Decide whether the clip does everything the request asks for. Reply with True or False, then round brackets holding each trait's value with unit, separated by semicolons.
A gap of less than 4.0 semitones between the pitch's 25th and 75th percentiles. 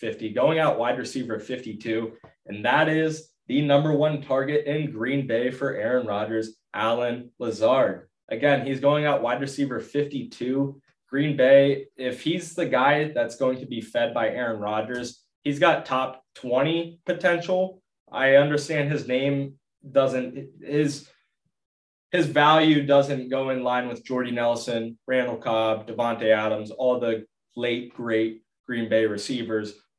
True (3.6 semitones)